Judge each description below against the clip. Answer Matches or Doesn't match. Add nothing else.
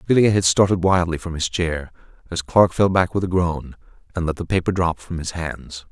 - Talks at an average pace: Doesn't match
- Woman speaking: Doesn't match